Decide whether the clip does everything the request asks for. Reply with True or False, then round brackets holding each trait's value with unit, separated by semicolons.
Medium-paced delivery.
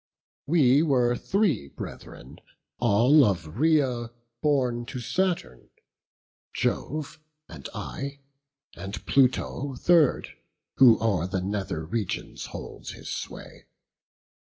False (100 wpm)